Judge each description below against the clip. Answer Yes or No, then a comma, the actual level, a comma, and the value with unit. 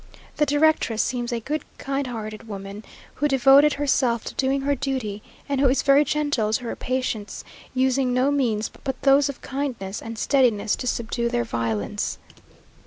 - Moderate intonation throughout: Yes, average, 3.7 semitones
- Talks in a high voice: Yes, very high, 255 Hz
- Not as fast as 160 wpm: No, average, 170 wpm